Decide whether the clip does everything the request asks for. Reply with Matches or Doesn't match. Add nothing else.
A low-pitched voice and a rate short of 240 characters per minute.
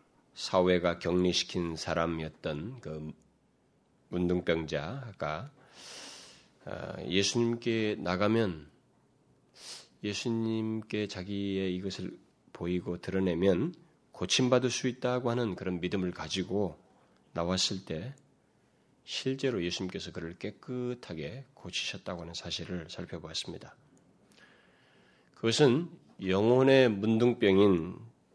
Matches